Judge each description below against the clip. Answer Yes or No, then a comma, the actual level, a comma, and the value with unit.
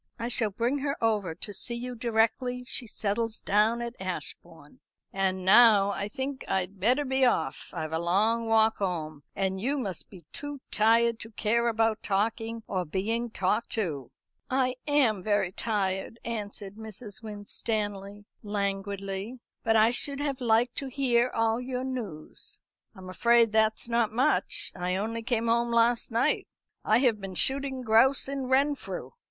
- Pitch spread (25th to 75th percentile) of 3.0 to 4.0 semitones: Yes, average, 3.4 semitones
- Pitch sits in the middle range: No, high, 225 Hz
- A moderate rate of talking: Yes, average, 160 wpm